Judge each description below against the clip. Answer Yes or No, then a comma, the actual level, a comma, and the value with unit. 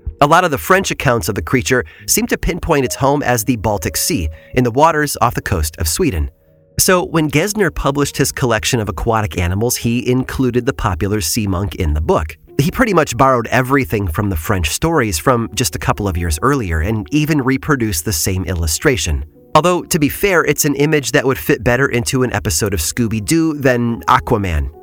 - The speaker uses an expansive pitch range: Yes, wide, 6.6 semitones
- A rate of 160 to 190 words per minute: No, fast, 205 wpm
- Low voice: Yes, low, 120 Hz